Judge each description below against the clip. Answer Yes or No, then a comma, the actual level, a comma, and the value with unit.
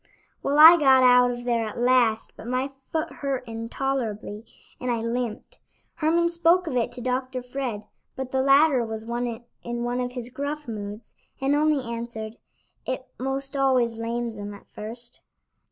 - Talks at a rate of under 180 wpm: Yes, average, 165 wpm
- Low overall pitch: No, very high, 250 Hz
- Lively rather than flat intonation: No, average, 2.7 semitones